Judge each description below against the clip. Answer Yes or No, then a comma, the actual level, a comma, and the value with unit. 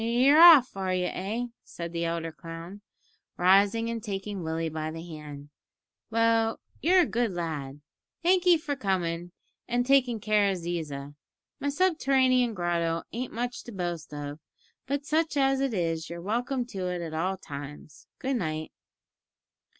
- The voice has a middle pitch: No, high, 195 Hz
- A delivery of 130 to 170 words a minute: Yes, average, 160 wpm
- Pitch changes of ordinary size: No, wide, 6.9 semitones